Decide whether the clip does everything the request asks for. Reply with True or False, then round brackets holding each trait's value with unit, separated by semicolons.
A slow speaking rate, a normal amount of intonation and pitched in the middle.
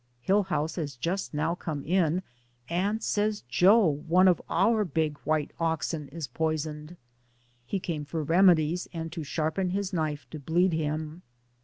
False (150 wpm; 3.1 semitones; 165 Hz)